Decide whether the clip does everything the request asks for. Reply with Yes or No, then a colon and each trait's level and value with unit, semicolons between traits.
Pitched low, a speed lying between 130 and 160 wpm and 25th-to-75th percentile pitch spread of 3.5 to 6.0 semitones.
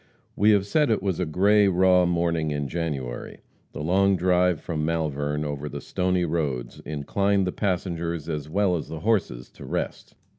No: very low, 85 Hz; average, 175 wpm; average, 3.8 semitones